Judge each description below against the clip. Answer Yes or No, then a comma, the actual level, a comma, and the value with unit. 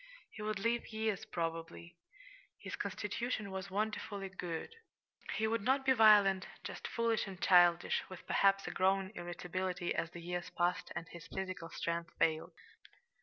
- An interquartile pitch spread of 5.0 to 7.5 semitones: No, average, 3.6 semitones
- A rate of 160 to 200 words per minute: No, average, 150 wpm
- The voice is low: No, high, 190 Hz